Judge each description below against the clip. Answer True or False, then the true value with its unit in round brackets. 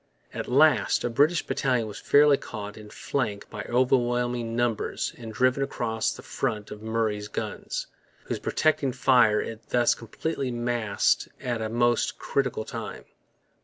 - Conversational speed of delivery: True (145 wpm)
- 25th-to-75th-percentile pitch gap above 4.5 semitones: False (2.6 semitones)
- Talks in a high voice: False (120 Hz)